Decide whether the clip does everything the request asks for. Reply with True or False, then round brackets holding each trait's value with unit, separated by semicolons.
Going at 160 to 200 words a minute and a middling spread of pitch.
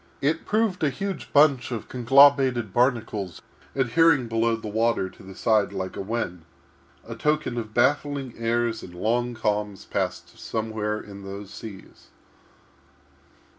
False (135 wpm; 4.3 semitones)